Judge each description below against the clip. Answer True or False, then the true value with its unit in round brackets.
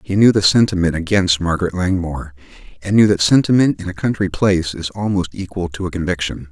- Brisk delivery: False (195 wpm)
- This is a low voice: True (90 Hz)